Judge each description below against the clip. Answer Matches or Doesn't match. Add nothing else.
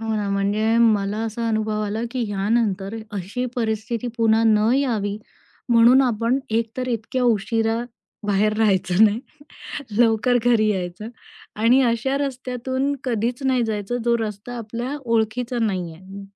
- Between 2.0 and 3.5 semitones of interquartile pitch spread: Matches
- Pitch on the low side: Doesn't match